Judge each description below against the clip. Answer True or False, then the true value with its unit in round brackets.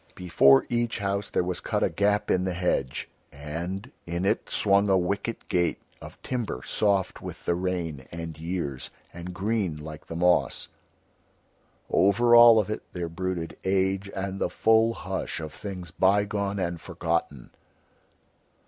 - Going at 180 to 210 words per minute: False (150 wpm)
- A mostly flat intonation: False (3.1 semitones)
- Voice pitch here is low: True (95 Hz)